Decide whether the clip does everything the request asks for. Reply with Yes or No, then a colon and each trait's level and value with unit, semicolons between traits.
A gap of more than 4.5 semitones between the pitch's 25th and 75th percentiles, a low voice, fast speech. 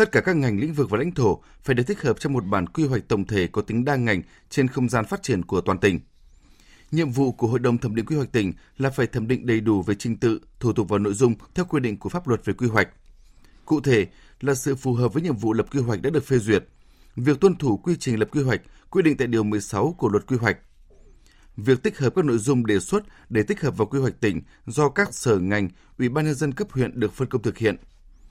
Yes: average, 5.1 semitones; low, 120 Hz; fast, 270 wpm